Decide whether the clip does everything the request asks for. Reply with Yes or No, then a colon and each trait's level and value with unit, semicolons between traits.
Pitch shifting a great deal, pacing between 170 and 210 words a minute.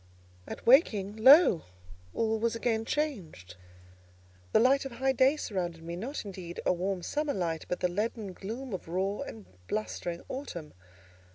No: wide, 6.5 semitones; average, 155 wpm